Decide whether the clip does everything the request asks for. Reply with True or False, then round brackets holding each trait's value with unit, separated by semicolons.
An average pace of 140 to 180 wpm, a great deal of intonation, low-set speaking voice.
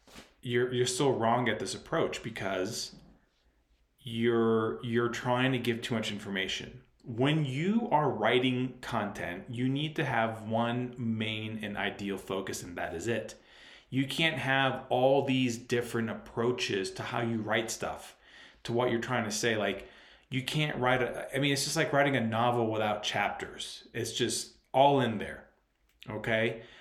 False (165 wpm; 2.6 semitones; 120 Hz)